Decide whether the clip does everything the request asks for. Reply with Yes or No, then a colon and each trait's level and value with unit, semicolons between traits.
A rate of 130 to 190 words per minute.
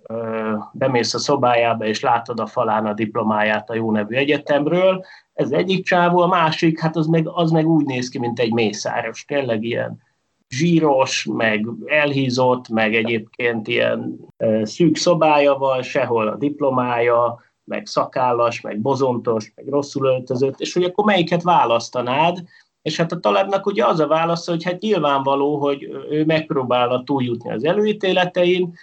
Yes: average, 150 wpm